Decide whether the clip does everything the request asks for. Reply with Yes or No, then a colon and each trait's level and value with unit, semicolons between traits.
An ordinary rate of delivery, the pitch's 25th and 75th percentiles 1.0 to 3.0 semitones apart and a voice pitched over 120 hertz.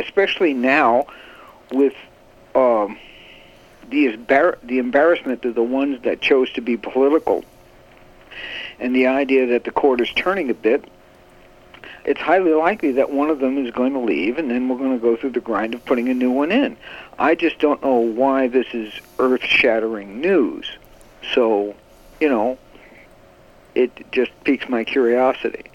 Yes: average, 160 wpm; narrow, 2.6 semitones; low, 130 Hz